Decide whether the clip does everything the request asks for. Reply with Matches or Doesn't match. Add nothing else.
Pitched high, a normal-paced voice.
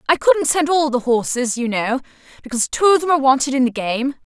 Doesn't match